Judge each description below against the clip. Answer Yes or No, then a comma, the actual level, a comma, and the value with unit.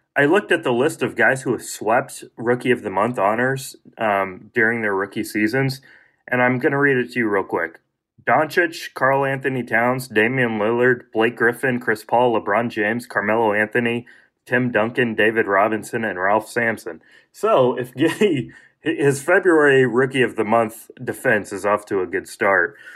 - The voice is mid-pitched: No, low, 125 Hz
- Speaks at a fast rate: No, average, 175 wpm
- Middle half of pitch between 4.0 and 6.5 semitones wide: No, average, 3.1 semitones